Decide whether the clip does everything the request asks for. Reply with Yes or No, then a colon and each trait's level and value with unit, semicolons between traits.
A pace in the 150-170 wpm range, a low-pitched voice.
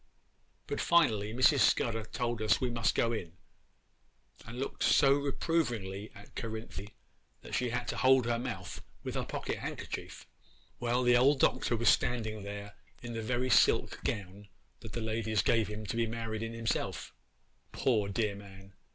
Yes: average, 165 wpm; low, 115 Hz